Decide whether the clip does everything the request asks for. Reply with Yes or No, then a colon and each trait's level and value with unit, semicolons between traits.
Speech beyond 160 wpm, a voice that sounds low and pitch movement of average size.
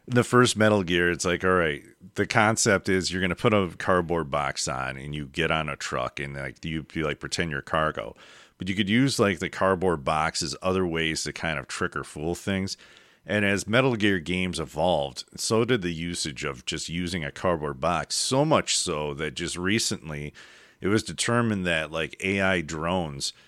Yes: fast, 205 wpm; very low, 90 Hz; average, 4.1 semitones